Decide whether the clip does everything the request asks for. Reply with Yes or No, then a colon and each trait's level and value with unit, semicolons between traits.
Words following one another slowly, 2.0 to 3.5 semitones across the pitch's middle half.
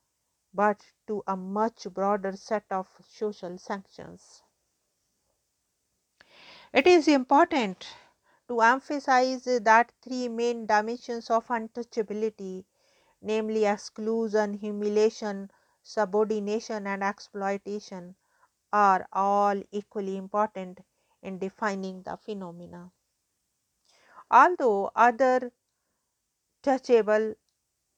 Yes: slow, 80 wpm; average, 2.8 semitones